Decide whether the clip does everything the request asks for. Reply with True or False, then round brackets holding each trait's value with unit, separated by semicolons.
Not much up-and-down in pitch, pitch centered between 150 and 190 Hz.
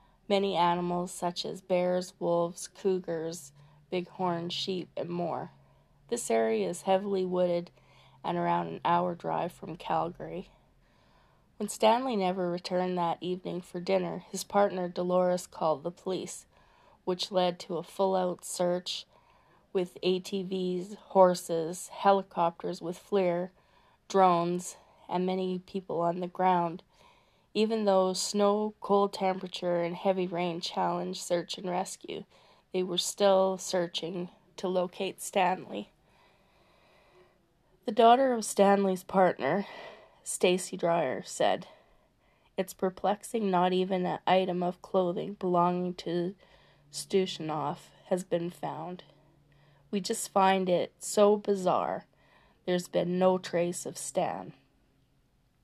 True (1.7 semitones; 185 Hz)